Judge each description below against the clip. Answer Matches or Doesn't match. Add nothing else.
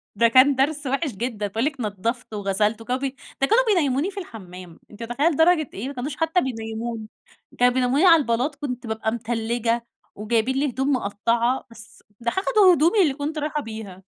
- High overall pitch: Matches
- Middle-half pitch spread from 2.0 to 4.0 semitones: Doesn't match